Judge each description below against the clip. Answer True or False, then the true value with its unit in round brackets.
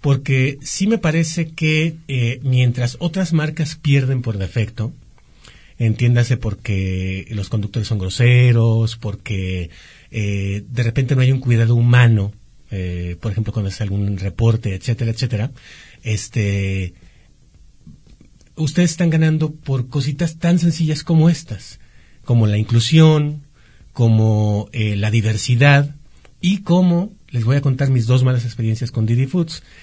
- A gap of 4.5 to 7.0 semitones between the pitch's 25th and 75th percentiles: True (5.2 semitones)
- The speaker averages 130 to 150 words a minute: True (135 wpm)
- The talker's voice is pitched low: True (120 Hz)